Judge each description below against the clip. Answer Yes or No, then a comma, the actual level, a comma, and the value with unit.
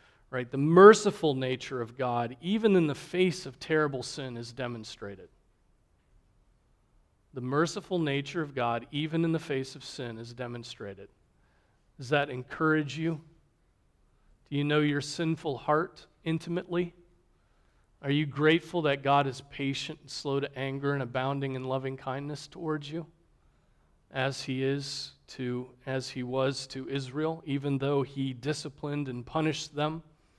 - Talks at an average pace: Yes, average, 145 wpm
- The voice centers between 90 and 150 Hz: Yes, medium, 140 Hz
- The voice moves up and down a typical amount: Yes, average, 3.2 semitones